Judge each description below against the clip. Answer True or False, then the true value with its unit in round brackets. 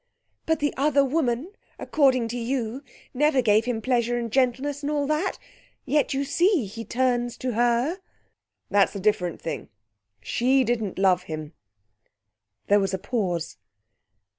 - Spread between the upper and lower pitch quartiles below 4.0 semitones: False (4.8 semitones)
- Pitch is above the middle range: True (245 Hz)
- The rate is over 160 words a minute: False (145 wpm)